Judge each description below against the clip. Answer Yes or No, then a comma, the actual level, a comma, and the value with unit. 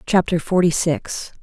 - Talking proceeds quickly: No, slow, 125 wpm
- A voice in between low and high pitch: Yes, medium, 170 Hz